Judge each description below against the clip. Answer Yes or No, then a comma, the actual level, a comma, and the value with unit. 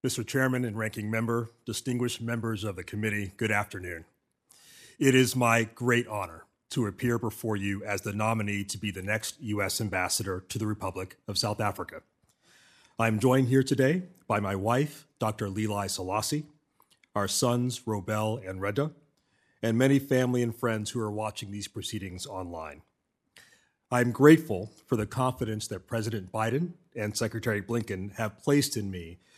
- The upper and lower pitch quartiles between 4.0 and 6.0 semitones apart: No, average, 3.2 semitones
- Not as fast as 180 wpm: Yes, average, 160 wpm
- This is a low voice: Yes, low, 110 Hz